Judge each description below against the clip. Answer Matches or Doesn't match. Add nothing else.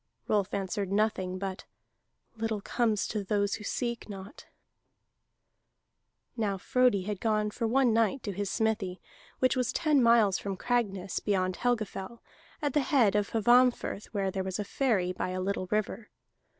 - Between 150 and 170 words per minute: Matches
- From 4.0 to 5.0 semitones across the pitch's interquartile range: Doesn't match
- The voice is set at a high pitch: Matches